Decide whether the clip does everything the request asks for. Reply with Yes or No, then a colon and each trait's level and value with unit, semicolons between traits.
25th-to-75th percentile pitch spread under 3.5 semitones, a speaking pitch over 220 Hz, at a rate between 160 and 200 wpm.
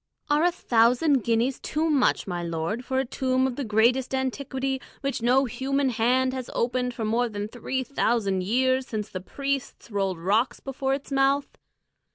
Yes: average, 3.1 semitones; very high, 255 Hz; average, 175 wpm